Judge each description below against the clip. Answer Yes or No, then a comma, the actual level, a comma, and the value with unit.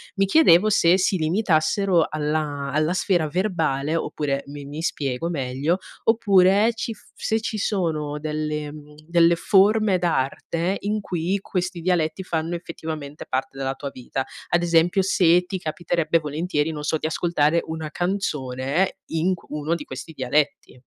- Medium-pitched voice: Yes, medium, 165 Hz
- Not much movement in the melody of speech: No, average, 3.5 semitones